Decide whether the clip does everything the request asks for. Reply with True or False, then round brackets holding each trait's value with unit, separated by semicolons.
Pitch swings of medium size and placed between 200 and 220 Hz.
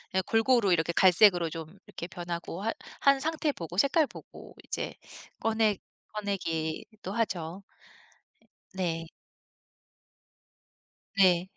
False (4.7 semitones; 190 Hz)